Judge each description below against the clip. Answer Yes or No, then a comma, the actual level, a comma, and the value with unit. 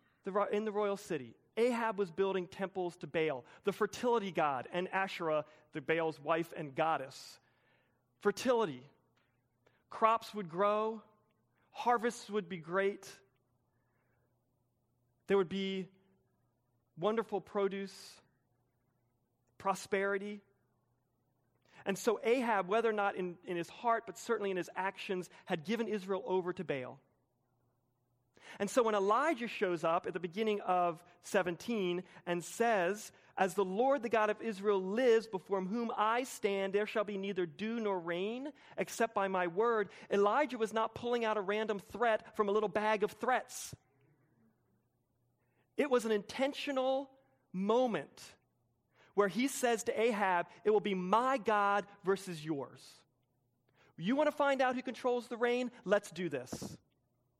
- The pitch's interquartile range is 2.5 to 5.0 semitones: No, wide, 5.5 semitones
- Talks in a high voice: Yes, high, 195 Hz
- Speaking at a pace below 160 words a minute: Yes, average, 140 wpm